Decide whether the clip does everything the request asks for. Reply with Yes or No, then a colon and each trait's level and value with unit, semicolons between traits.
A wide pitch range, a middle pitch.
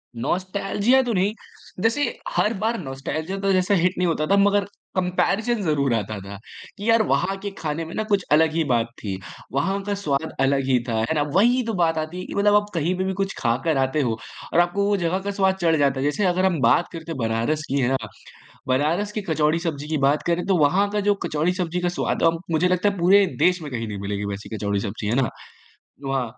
Yes: wide, 6.0 semitones; medium, 170 Hz